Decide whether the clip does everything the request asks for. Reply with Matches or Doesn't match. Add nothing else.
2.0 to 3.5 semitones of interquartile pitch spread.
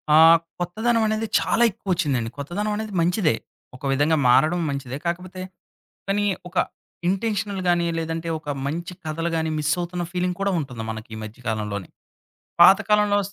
Doesn't match